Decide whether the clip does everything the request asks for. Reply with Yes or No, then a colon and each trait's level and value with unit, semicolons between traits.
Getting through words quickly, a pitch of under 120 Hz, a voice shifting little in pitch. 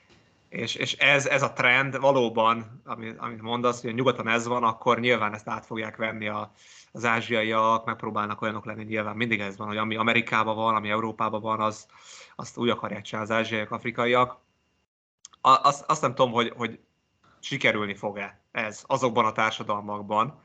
Yes: fast, 170 wpm; low, 110 Hz; narrow, 1.8 semitones